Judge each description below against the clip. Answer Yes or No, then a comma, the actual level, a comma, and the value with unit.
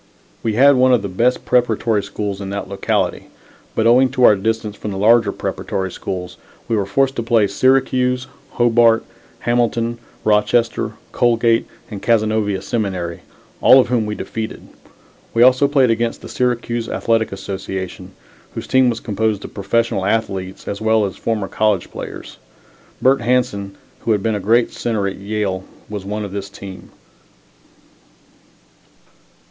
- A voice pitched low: Yes, low, 110 Hz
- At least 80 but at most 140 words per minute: No, average, 155 wpm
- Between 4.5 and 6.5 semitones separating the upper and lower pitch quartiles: No, average, 3.1 semitones